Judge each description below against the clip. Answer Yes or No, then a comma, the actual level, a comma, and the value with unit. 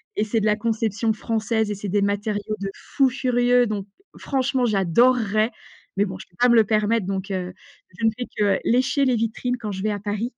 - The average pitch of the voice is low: No, high, 215 Hz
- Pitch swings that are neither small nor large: Yes, average, 3.0 semitones